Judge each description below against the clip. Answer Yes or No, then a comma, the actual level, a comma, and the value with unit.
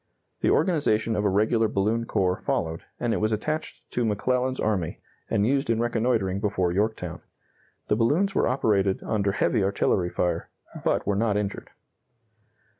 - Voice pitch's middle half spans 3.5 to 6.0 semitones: No, average, 3.1 semitones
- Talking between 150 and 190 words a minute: Yes, average, 155 wpm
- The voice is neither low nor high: No, low, 110 Hz